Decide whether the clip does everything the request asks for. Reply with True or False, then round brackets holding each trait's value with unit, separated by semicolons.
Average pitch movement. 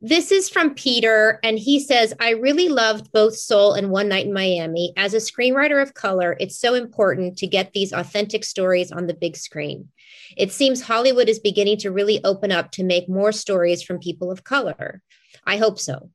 True (3.8 semitones)